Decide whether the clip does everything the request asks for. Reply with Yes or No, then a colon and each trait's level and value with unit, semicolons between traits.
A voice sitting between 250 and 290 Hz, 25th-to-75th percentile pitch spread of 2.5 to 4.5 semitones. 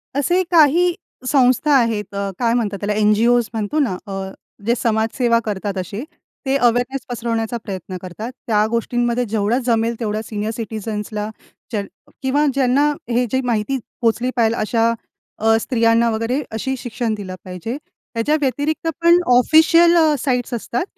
No: high, 235 Hz; average, 3.3 semitones